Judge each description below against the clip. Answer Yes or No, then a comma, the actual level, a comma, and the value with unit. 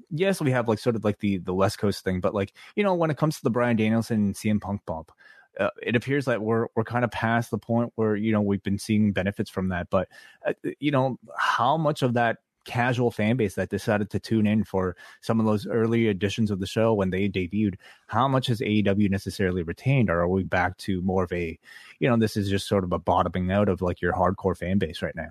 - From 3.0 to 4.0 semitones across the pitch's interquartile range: Yes, average, 3.4 semitones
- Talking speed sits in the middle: No, fast, 255 wpm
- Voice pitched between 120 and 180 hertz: No, low, 105 Hz